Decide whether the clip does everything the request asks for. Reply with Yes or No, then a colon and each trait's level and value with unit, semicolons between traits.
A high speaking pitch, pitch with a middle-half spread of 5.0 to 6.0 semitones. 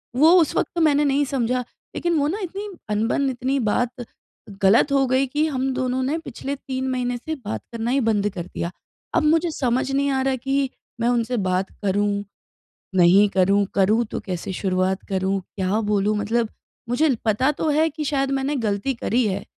Yes: very high, 250 Hz; average, 5.3 semitones